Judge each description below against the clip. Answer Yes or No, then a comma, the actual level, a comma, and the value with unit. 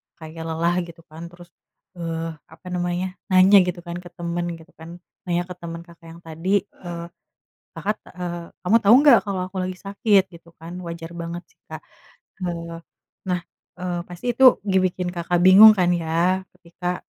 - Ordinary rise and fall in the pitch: No, narrow, 1.6 semitones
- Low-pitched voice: No, medium, 175 Hz